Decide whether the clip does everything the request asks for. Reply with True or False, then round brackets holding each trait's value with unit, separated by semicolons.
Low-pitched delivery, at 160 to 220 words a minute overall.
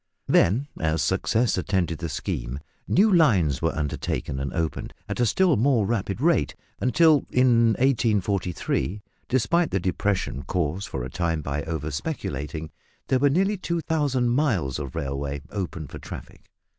False (95 Hz; 145 wpm)